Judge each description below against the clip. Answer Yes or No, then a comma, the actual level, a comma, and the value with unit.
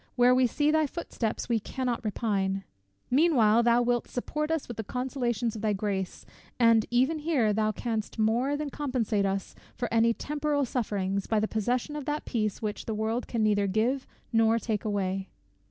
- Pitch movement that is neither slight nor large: Yes, average, 3.3 semitones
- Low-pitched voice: No, high, 230 Hz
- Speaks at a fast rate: No, average, 185 wpm